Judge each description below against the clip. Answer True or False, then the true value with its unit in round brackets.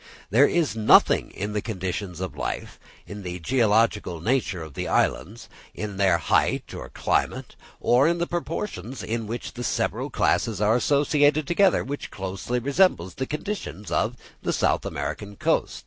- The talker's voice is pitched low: True (110 Hz)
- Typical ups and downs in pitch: False (6.5 semitones)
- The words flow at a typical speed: True (160 wpm)